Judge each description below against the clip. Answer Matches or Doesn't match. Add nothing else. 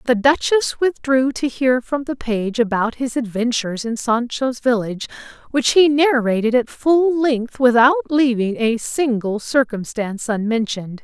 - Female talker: Matches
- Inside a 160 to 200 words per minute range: Doesn't match